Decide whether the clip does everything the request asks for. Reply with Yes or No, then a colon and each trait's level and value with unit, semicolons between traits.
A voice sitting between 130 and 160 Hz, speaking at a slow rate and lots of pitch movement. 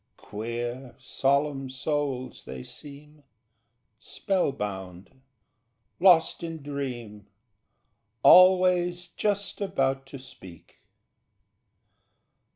Yes: medium, 140 Hz; slow, 70 wpm; wide, 5.8 semitones